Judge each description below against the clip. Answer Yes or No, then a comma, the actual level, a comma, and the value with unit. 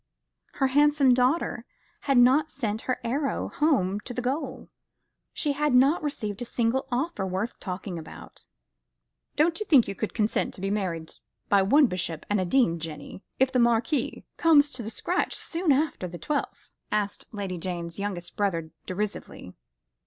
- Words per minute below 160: No, average, 165 wpm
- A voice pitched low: No, high, 235 Hz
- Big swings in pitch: Yes, wide, 6.7 semitones